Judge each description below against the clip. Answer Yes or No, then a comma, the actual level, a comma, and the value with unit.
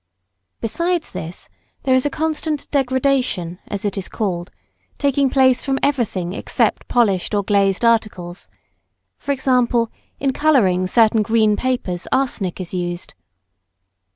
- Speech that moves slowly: Yes, slow, 125 wpm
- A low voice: No, high, 225 Hz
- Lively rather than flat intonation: Yes, wide, 6.3 semitones